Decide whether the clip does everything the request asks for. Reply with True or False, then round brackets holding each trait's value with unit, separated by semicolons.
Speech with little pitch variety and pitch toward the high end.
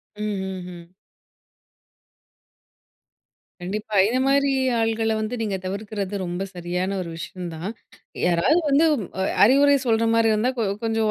False (3.6 semitones; 210 Hz)